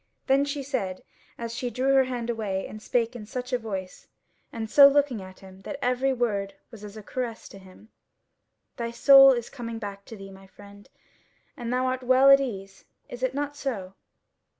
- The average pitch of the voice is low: No, high, 235 Hz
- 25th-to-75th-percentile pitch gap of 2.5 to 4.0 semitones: No, average, 4.4 semitones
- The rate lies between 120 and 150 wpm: No, average, 195 wpm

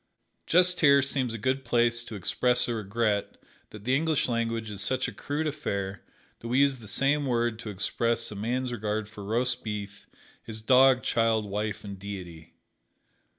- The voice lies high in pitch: No, low, 115 Hz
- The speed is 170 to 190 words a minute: Yes, average, 175 wpm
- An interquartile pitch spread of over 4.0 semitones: No, average, 3.7 semitones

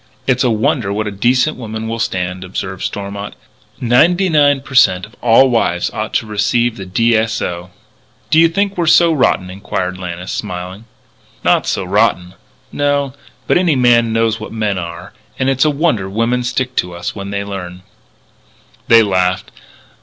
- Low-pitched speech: Yes, low, 110 Hz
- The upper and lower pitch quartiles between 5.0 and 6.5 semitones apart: Yes, wide, 5.4 semitones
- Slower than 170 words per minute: No, average, 175 wpm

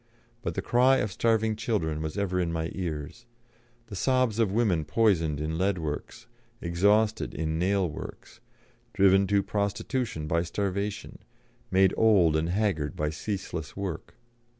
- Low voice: Yes, very low, 95 Hz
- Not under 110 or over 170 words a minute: Yes, average, 145 wpm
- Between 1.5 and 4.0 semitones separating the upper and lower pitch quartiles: No, average, 4.9 semitones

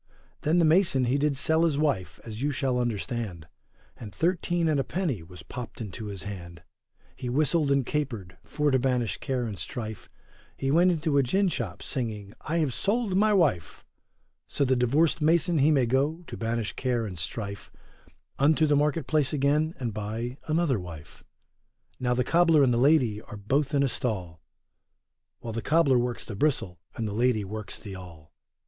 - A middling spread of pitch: No, wide, 5.8 semitones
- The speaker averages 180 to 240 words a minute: Yes, average, 185 wpm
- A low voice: Yes, low, 130 Hz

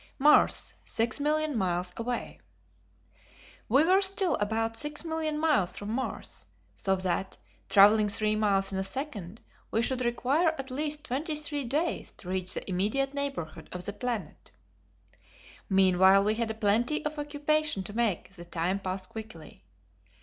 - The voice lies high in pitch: Yes, high, 225 Hz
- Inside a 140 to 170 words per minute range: Yes, average, 145 wpm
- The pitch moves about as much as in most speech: No, wide, 7.2 semitones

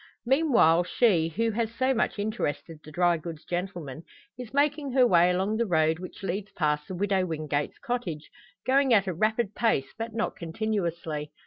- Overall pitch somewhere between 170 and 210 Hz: Yes, high, 190 Hz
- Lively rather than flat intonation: Yes, wide, 5.8 semitones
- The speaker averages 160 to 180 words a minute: Yes, average, 175 wpm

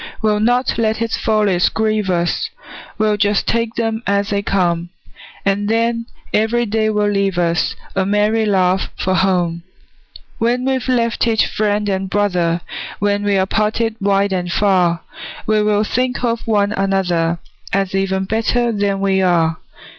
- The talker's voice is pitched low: No, high, 205 Hz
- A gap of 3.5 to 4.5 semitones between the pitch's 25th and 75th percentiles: No, narrow, 2.5 semitones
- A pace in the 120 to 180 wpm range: Yes, average, 155 wpm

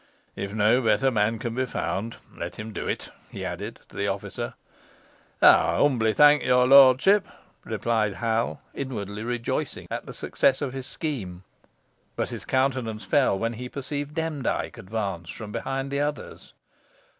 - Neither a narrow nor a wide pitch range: Yes, average, 4.0 semitones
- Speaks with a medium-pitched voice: No, low, 120 Hz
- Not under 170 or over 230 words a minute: No, average, 155 wpm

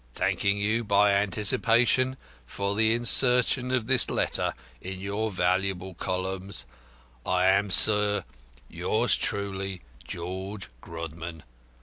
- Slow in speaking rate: Yes, slow, 105 wpm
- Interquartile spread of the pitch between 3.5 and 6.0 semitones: No, average, 2.8 semitones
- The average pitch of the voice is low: Yes, low, 100 Hz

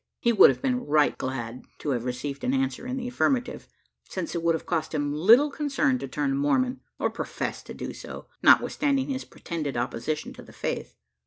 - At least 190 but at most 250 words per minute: Yes, average, 195 wpm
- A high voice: No, medium, 165 Hz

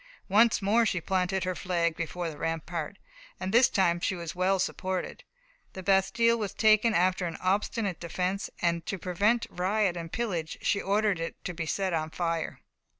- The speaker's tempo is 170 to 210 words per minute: Yes, average, 175 wpm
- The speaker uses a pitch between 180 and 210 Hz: Yes, medium, 185 Hz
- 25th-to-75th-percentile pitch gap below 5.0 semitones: Yes, average, 2.9 semitones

